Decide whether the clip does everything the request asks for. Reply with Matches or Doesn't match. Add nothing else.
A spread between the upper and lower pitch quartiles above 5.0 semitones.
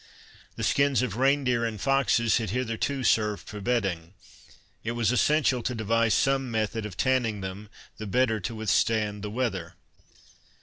Doesn't match